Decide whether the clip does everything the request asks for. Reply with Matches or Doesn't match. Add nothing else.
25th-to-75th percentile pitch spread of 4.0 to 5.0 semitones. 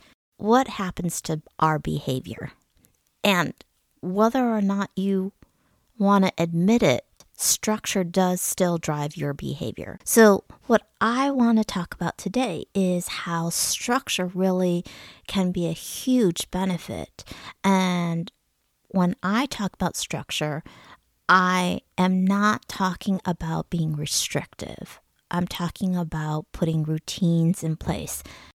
Doesn't match